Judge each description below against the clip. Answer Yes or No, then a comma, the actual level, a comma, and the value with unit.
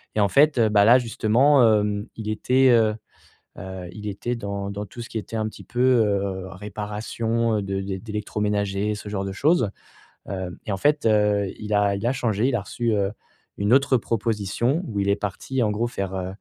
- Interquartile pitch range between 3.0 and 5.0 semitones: No, narrow, 2.6 semitones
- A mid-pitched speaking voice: No, low, 105 Hz